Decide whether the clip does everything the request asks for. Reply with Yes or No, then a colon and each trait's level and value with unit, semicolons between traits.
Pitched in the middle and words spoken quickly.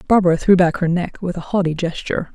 Yes: medium, 175 Hz; fast, 230 wpm